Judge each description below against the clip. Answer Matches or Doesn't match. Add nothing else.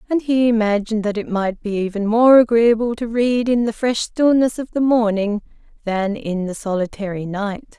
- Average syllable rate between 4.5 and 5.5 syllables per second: Matches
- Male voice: Doesn't match